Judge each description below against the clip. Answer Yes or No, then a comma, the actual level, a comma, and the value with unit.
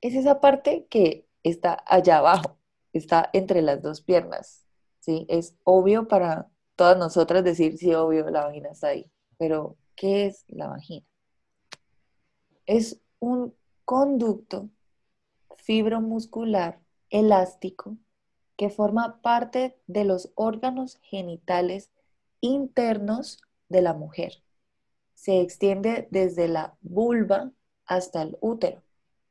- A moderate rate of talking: No, slow, 110 wpm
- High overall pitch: Yes, high, 195 Hz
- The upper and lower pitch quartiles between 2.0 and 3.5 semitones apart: No, average, 4.7 semitones